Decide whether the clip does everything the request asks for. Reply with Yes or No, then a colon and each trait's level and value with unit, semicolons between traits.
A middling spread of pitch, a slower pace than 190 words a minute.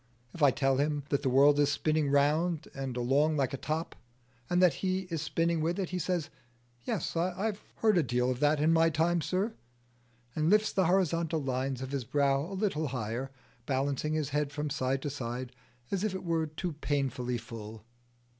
No: average, 3.9 semitones; average, 195 wpm